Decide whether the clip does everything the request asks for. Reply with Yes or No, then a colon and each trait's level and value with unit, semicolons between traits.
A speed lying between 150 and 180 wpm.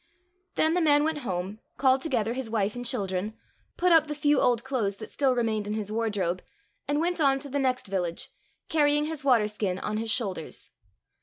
No: fast, 205 wpm